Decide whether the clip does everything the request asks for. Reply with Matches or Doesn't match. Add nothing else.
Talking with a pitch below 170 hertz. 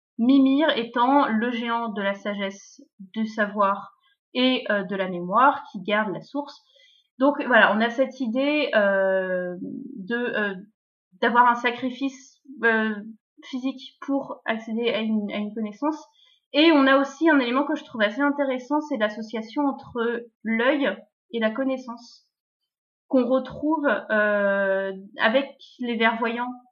Doesn't match